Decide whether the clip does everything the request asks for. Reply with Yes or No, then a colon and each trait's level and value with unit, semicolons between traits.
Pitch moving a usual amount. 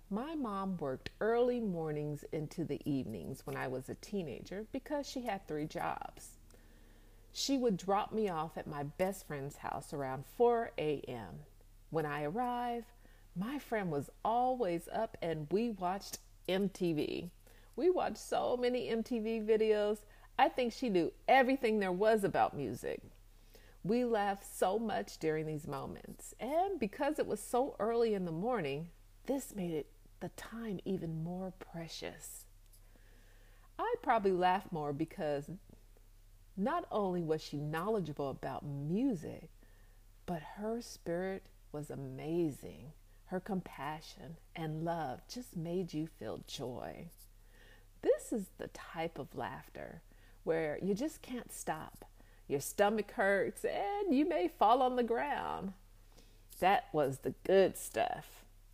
No: wide, 7.8 semitones